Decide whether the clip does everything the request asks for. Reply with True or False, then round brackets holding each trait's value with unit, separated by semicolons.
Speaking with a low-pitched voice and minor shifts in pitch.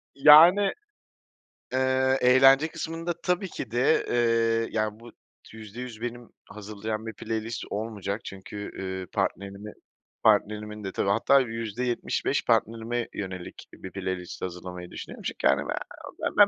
False (115 Hz; 3.8 semitones)